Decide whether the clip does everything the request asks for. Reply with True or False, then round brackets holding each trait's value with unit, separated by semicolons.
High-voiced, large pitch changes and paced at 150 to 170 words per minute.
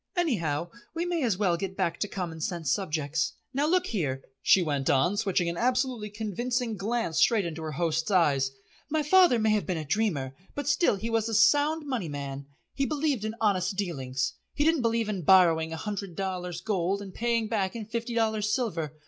False (200 Hz; 5.9 semitones; 200 wpm)